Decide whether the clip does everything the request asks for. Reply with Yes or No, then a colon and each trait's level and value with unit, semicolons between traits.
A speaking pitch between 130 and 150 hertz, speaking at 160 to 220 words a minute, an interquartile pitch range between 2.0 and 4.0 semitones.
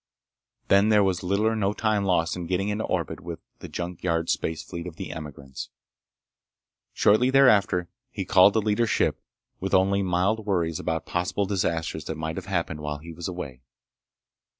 No: very low, 90 Hz; average, 175 wpm; average, 3.6 semitones